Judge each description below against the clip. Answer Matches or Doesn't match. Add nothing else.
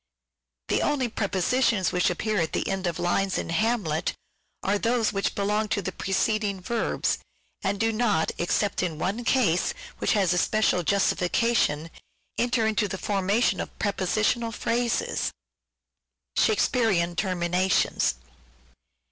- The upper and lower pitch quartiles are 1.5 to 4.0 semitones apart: Matches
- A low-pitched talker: Doesn't match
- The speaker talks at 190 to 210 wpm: Doesn't match